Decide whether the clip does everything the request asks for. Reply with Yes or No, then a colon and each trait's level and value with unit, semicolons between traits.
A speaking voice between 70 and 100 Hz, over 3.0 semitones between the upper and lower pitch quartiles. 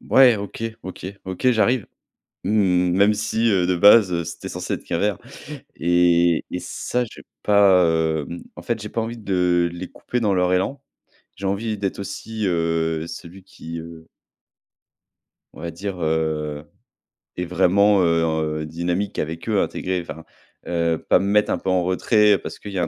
Yes: very low, 90 Hz; average, 3.4 semitones